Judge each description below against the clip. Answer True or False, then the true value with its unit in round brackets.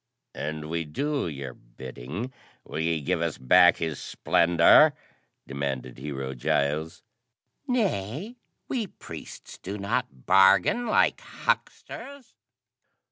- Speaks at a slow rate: True (105 wpm)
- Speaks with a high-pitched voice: False (80 Hz)